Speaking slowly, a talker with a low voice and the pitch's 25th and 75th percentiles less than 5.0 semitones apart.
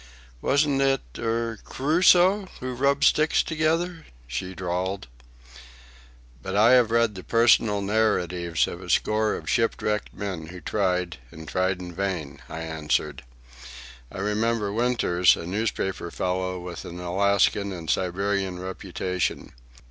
Yes: slow, 125 wpm; low, 100 Hz; average, 4.5 semitones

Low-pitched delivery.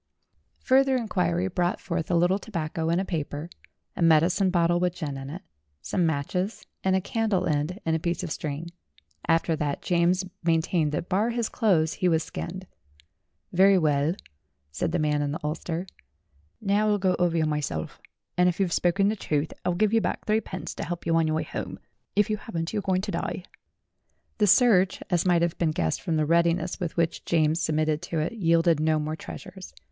No: medium, 170 Hz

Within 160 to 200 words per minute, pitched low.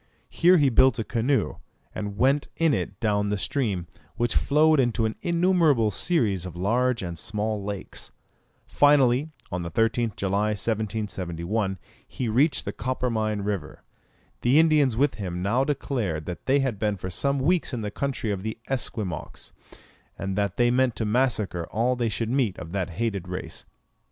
Yes: average, 165 wpm; low, 110 Hz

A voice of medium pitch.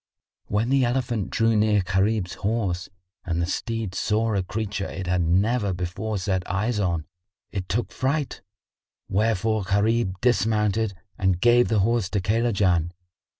No: low, 105 Hz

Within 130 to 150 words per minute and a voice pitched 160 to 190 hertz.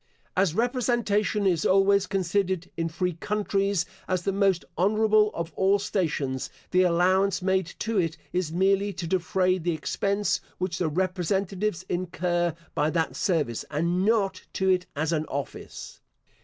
Yes: average, 145 wpm; medium, 185 Hz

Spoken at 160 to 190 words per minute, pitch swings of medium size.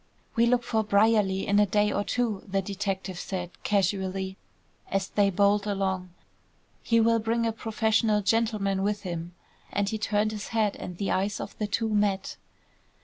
No: average, 170 wpm; narrow, 2.2 semitones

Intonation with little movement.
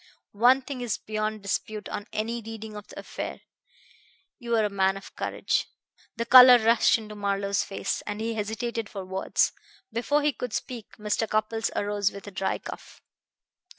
Yes: narrow, 2.3 semitones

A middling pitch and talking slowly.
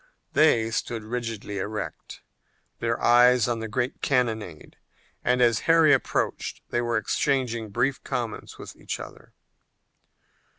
No: low, 120 Hz; slow, 125 wpm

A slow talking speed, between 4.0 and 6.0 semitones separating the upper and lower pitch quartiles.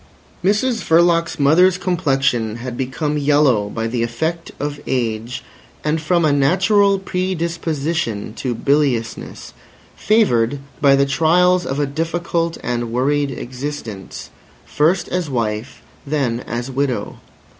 Yes: slow, 120 wpm; wide, 5.5 semitones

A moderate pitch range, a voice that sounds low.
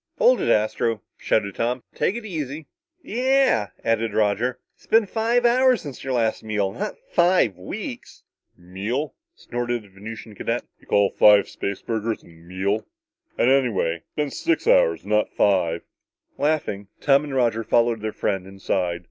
No: wide, 7.5 semitones; low, 115 Hz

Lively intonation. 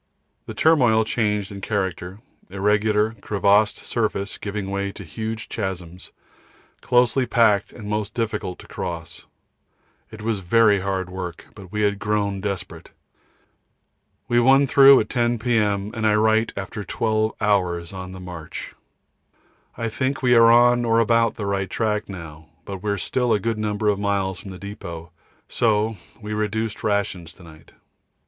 No: narrow, 2.6 semitones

